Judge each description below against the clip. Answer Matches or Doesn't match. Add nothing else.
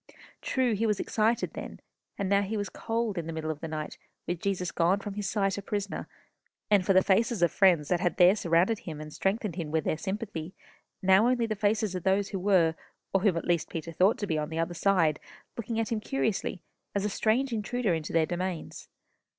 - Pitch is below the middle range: Doesn't match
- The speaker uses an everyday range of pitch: Matches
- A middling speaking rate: Doesn't match